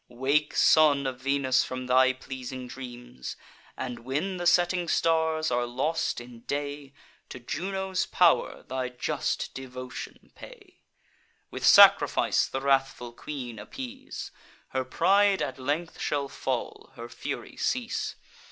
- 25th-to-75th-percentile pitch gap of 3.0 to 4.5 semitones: No, average, 5.0 semitones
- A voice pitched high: No, medium, 140 Hz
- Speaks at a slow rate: Yes, slow, 125 wpm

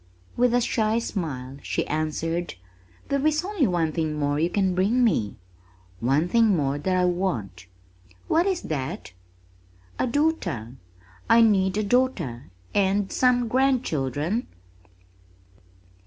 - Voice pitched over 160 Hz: Yes, medium, 185 Hz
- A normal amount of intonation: No, wide, 7.9 semitones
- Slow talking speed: Yes, slow, 125 wpm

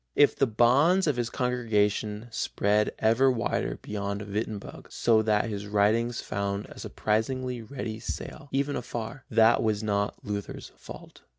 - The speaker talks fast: No, average, 140 wpm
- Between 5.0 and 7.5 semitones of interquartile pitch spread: No, average, 3.1 semitones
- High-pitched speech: No, low, 110 Hz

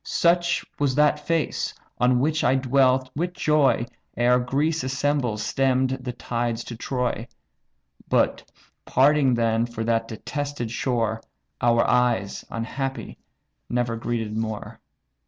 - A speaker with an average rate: No, slow, 120 wpm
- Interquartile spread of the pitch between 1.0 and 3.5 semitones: Yes, average, 3.2 semitones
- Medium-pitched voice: No, low, 125 Hz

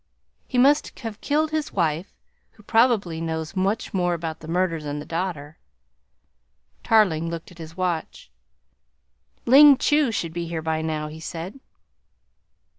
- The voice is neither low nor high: Yes, medium, 175 Hz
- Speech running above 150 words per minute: No, average, 145 wpm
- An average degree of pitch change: No, wide, 5.8 semitones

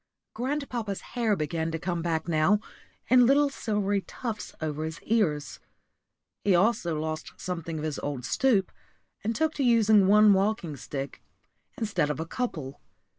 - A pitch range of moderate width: No, wide, 6.1 semitones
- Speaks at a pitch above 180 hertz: Yes, high, 190 Hz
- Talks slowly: No, average, 150 wpm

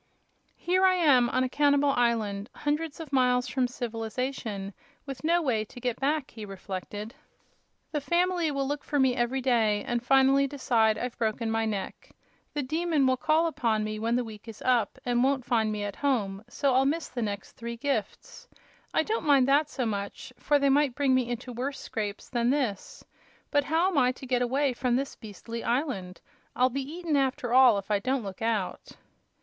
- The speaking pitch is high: Yes, very high, 255 Hz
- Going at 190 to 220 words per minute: Yes, average, 195 wpm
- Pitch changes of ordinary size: Yes, average, 3.9 semitones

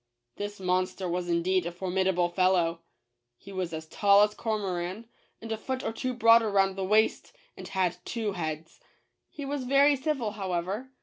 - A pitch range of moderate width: Yes, average, 3.8 semitones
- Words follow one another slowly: No, average, 170 wpm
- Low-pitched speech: No, high, 195 Hz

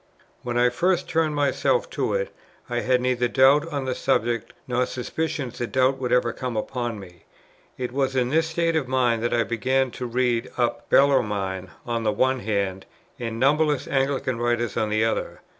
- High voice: No, low, 125 Hz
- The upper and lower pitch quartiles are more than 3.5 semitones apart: No, narrow, 2.5 semitones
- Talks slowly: No, average, 185 wpm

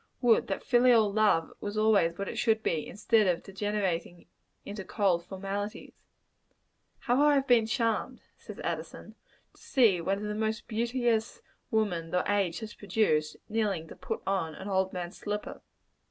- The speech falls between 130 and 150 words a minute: No, average, 160 wpm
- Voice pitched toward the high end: Yes, high, 205 Hz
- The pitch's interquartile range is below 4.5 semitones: Yes, average, 2.9 semitones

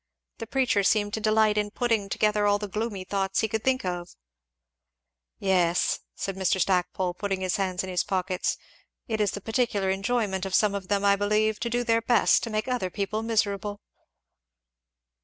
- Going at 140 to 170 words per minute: No, average, 180 wpm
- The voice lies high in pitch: Yes, high, 205 Hz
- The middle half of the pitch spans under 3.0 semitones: Yes, narrow, 2.4 semitones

